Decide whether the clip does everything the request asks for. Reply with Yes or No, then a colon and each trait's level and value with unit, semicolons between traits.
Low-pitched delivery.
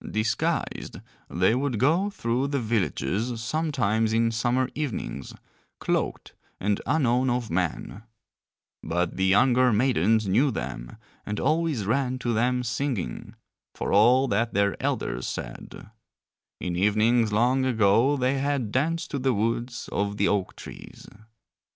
Yes: low, 115 Hz